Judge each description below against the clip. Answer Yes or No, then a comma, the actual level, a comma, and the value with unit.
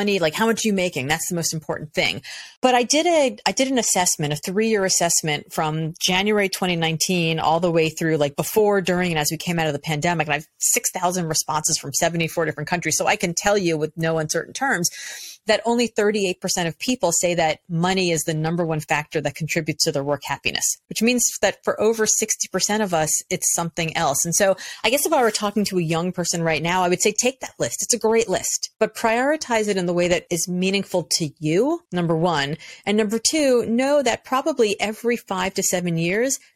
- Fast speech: Yes, fast, 225 wpm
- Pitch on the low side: No, medium, 180 Hz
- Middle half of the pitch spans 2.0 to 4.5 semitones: No, average, 5.0 semitones